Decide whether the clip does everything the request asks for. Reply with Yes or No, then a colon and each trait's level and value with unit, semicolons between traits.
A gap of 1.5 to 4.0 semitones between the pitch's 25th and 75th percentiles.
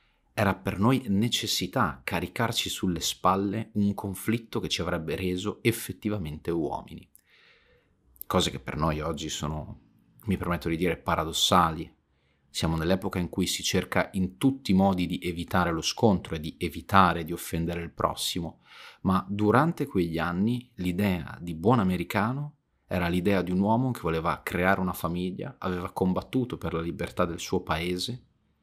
Yes: average, 3.3 semitones